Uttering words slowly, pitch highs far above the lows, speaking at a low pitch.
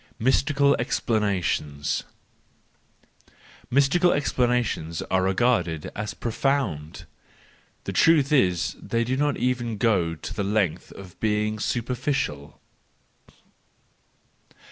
Yes: slow, 90 wpm; wide, 6.0 semitones; low, 110 Hz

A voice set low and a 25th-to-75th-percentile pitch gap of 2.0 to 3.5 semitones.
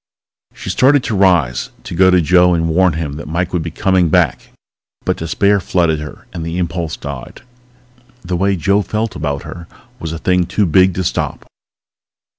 Yes: very low, 90 Hz; narrow, 2.6 semitones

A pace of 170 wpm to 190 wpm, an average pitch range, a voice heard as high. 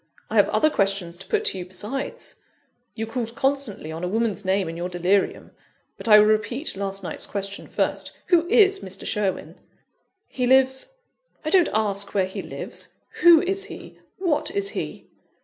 No: average, 180 wpm; wide, 6.7 semitones; high, 215 Hz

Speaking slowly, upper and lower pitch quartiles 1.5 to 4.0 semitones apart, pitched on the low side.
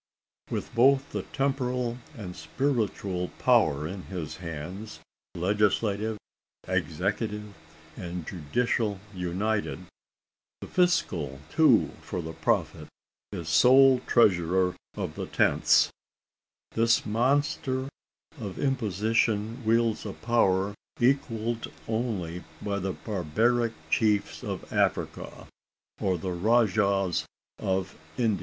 No: slow, 100 wpm; average, 4.5 semitones; low, 105 Hz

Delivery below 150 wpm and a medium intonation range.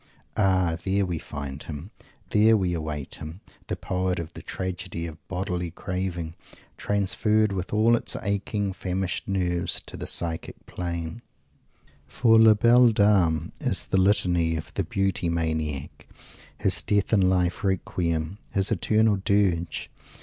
Yes: average, 140 wpm; average, 3.2 semitones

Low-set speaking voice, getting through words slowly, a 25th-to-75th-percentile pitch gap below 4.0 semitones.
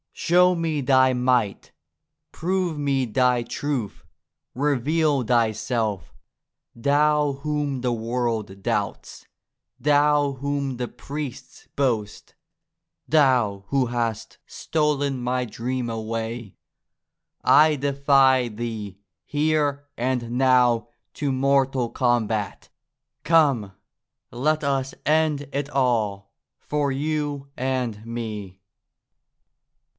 Yes: low, 130 Hz; slow, 90 wpm; average, 3.6 semitones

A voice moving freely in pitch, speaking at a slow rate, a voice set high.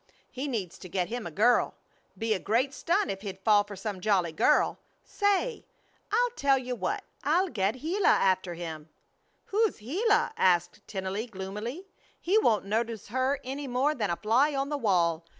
No: wide, 7.1 semitones; average, 175 wpm; high, 230 Hz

